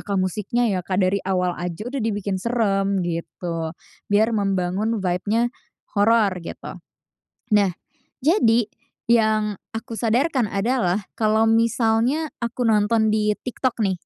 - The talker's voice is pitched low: No, high, 215 Hz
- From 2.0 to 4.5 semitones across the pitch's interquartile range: Yes, average, 3.1 semitones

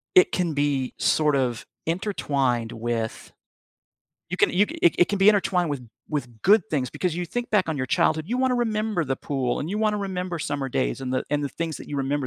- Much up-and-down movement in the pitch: Yes, wide, 6.4 semitones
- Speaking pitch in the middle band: Yes, medium, 155 Hz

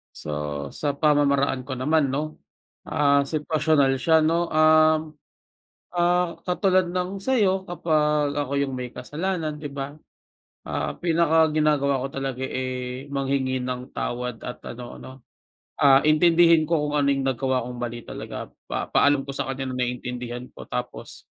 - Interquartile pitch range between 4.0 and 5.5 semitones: No, average, 3.4 semitones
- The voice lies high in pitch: No, medium, 145 Hz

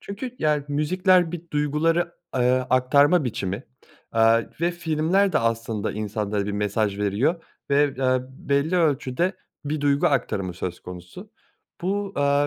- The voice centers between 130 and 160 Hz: Yes, medium, 140 Hz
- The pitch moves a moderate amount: No, wide, 7.0 semitones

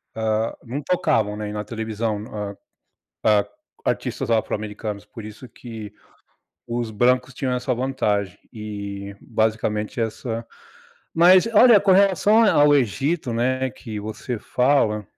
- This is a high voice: No, low, 115 Hz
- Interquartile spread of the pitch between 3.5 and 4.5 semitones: Yes, average, 3.8 semitones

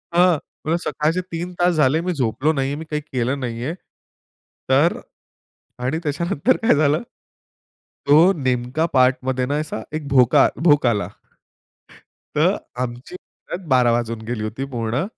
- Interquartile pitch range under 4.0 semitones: No, average, 4.3 semitones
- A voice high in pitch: No, medium, 140 Hz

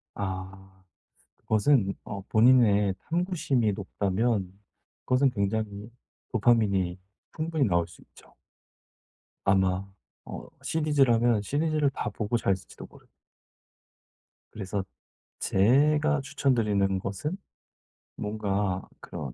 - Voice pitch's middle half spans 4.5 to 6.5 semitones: Yes, wide, 5.5 semitones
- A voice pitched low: Yes, low, 105 Hz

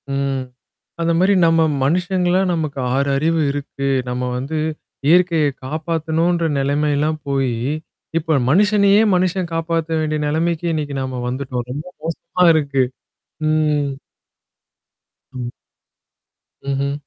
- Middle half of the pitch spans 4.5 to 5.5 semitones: No, average, 3.2 semitones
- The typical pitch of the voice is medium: Yes, medium, 155 Hz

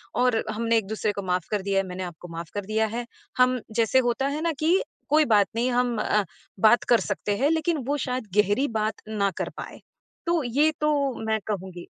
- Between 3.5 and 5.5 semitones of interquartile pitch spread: Yes, average, 4.0 semitones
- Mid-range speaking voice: No, high, 225 Hz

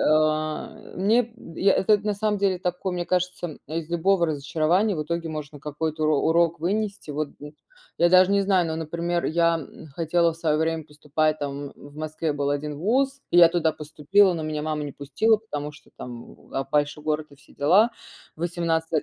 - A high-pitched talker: No, medium, 160 Hz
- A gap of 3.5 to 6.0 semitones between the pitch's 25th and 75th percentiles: No, average, 3.1 semitones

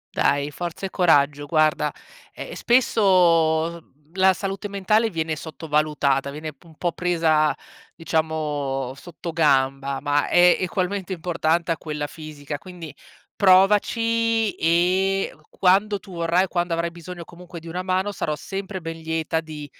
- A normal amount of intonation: Yes, average, 3.3 semitones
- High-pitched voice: No, medium, 165 Hz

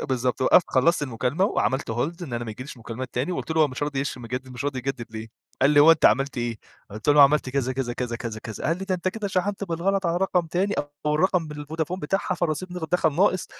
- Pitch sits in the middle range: Yes, medium, 145 Hz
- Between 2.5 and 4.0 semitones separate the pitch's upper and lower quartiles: No, wide, 5.5 semitones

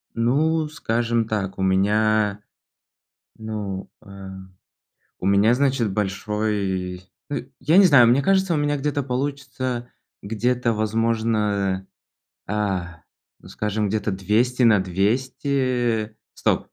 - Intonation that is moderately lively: Yes, average, 4.2 semitones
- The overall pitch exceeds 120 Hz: No, low, 110 Hz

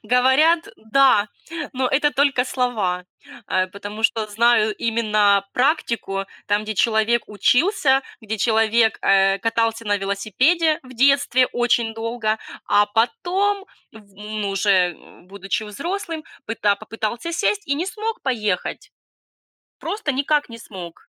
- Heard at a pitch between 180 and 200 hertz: No, high, 225 Hz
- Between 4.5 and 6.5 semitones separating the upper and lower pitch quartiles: Yes, average, 4.8 semitones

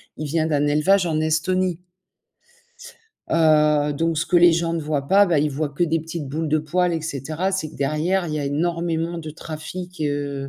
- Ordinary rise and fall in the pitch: No, narrow, 2.3 semitones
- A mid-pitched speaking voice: Yes, medium, 160 Hz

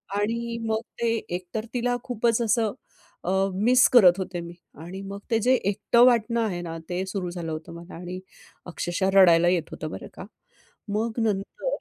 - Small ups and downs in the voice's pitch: No, average, 4.7 semitones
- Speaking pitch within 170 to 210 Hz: Yes, high, 195 Hz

